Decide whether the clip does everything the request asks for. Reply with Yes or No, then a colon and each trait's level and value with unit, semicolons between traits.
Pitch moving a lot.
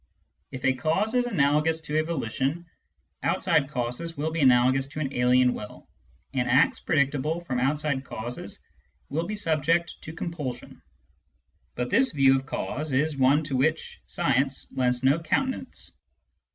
No: average, 3.8 semitones